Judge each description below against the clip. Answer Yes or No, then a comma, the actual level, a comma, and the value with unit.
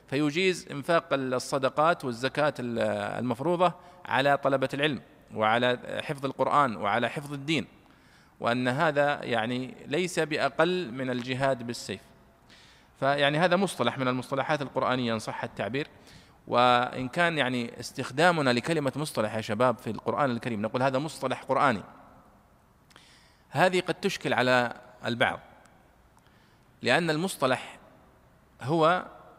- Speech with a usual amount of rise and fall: Yes, average, 3.9 semitones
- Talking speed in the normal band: Yes, average, 110 wpm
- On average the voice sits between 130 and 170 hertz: Yes, low, 135 Hz